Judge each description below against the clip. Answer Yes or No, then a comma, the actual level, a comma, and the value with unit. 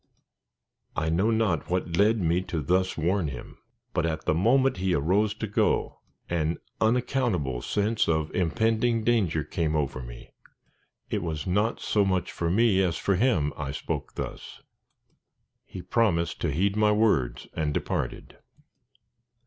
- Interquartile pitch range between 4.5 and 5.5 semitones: Yes, average, 5.2 semitones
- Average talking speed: Yes, average, 150 wpm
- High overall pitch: No, very low, 90 Hz